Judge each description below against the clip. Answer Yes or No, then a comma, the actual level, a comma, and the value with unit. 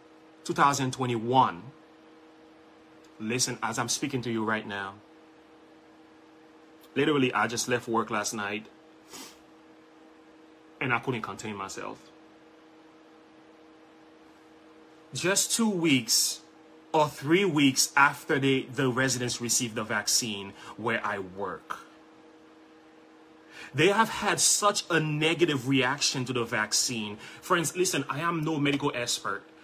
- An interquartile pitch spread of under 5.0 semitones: Yes, average, 4.5 semitones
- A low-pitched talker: No, medium, 155 Hz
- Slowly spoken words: Yes, slow, 110 wpm